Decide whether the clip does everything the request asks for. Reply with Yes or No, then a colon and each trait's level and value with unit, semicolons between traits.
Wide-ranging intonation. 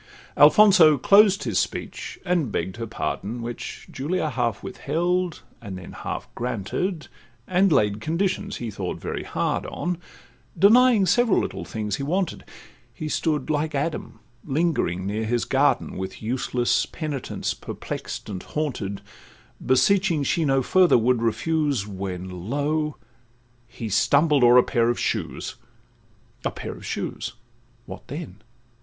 Yes: wide, 6.3 semitones